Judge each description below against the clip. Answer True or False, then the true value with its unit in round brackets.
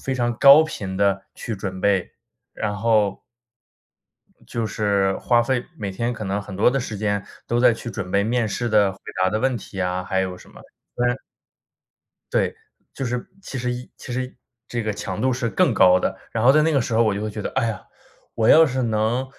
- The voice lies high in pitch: False (110 Hz)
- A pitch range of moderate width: True (3.6 semitones)